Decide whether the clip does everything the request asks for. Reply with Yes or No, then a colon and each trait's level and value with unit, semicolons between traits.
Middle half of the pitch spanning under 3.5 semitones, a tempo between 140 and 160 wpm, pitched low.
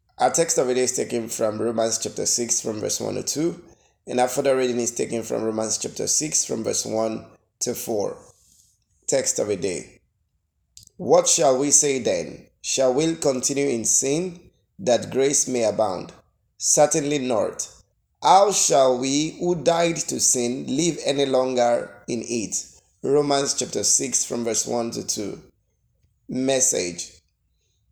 No: average, 4.5 semitones; average, 155 wpm; low, 125 Hz